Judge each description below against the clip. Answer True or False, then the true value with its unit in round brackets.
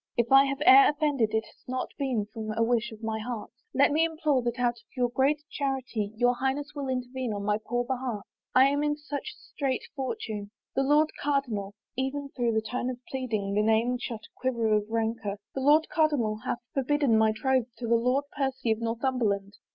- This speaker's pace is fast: True (215 wpm)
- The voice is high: True (250 Hz)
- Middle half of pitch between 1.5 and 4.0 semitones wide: True (3.6 semitones)